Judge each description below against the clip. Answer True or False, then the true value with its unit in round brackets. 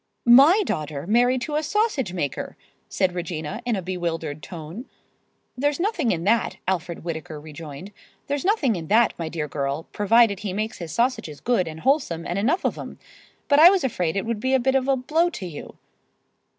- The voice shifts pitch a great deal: True (8.1 semitones)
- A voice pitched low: False (205 Hz)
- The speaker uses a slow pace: False (190 wpm)